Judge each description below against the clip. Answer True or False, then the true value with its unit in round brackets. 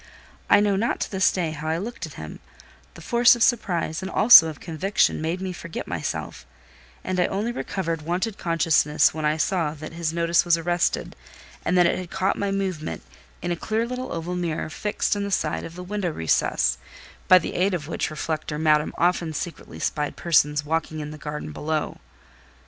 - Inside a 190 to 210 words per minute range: True (195 wpm)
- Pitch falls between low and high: True (170 Hz)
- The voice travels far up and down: False (3.4 semitones)